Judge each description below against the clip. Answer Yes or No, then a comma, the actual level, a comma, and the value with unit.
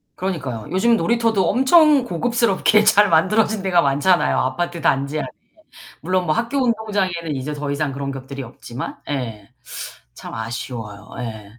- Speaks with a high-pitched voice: No, medium, 165 Hz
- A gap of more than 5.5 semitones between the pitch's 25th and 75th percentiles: Yes, wide, 8.0 semitones